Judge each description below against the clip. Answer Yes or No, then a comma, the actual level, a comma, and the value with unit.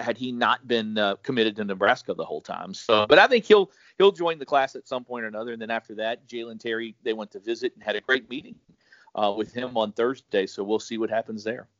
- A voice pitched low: Yes, low, 115 Hz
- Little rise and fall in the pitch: No, average, 3.1 semitones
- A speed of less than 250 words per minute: No, fast, 260 wpm